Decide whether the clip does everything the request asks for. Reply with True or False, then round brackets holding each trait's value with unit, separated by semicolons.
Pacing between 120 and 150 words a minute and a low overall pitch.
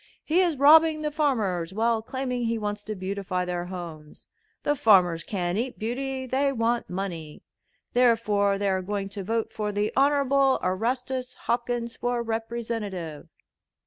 False (145 wpm; 225 Hz)